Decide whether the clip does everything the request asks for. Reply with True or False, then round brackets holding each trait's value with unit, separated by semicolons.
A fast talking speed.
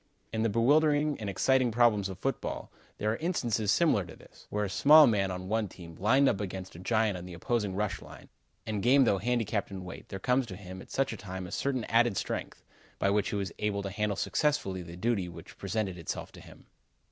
True (225 wpm)